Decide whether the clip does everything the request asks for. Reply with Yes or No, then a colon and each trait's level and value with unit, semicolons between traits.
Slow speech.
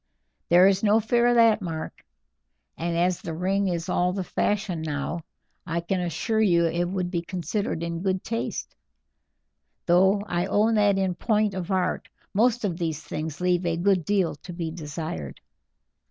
No: average, 170 wpm